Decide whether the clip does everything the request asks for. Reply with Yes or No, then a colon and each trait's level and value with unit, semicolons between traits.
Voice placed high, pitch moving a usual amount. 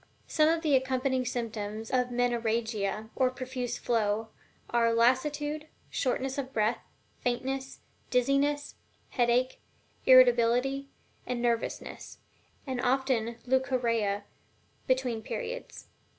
No: very high, 250 Hz; narrow, 2.3 semitones